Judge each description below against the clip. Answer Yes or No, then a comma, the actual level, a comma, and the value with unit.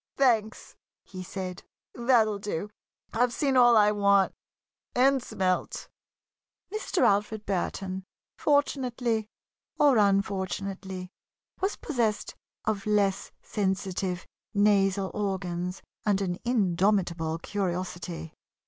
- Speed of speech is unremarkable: No, slow, 95 wpm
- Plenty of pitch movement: No, average, 3.0 semitones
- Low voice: No, high, 200 Hz